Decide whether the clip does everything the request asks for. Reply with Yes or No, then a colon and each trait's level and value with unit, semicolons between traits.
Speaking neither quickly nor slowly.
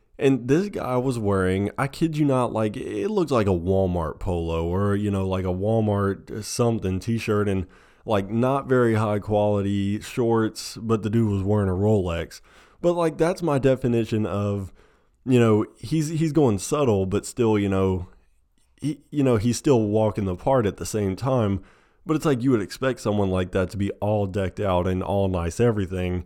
Yes: average, 190 wpm